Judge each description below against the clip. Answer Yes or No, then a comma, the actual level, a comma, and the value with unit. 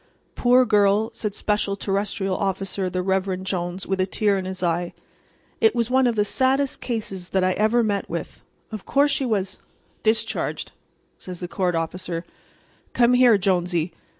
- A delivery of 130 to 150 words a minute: No, average, 165 wpm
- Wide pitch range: No, average, 3.2 semitones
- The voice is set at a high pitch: Yes, high, 195 Hz